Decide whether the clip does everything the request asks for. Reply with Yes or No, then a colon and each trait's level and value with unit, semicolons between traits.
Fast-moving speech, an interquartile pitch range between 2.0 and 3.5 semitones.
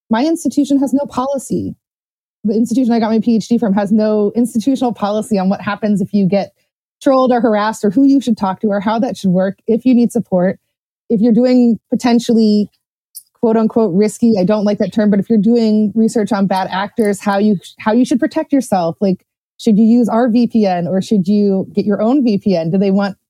Yes: fast, 215 wpm; average, 2.8 semitones